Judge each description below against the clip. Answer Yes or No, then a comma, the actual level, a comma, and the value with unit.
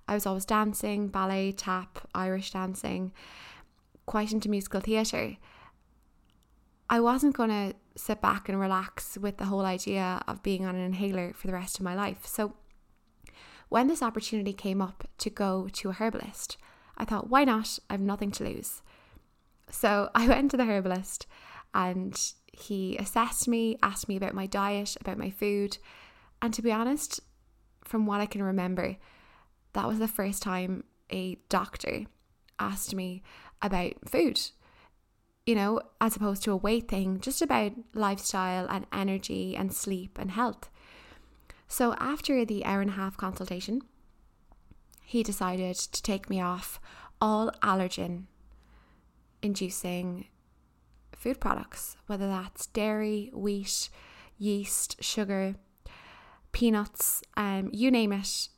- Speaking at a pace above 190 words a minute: No, average, 145 wpm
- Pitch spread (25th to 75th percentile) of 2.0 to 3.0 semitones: Yes, narrow, 2.6 semitones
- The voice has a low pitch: No, high, 200 Hz